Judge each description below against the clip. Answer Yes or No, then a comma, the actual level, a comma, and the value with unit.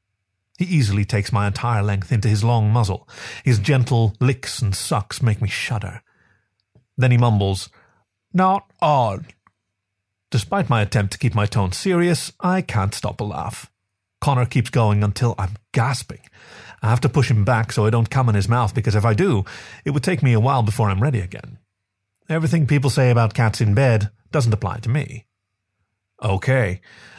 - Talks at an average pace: Yes, average, 180 wpm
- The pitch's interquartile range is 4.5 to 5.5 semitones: No, average, 3.9 semitones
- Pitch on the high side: No, low, 110 Hz